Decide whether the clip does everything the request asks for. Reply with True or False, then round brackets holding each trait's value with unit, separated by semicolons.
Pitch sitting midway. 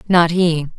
True (170 Hz)